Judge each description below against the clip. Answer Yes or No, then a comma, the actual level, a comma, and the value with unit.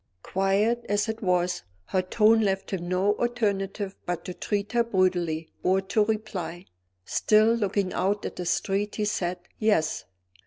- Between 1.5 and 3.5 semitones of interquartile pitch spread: Yes, average, 2.7 semitones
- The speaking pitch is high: Yes, high, 195 Hz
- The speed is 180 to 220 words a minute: No, average, 155 wpm